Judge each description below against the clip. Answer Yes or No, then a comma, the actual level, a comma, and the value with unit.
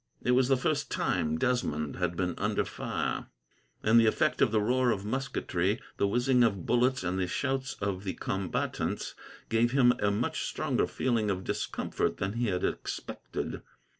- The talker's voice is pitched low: Yes, low, 110 Hz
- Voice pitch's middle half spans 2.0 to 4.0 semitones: No, average, 4.7 semitones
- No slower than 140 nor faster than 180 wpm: Yes, average, 170 wpm